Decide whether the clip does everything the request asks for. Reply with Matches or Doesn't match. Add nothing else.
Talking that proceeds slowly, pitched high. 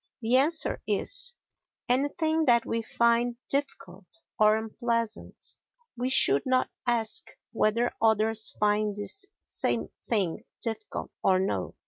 Matches